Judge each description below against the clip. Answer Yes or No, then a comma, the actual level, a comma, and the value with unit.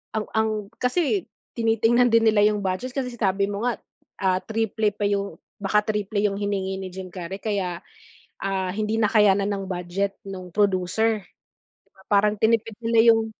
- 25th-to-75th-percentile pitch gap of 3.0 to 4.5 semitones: No, narrow, 2.4 semitones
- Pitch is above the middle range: Yes, high, 205 Hz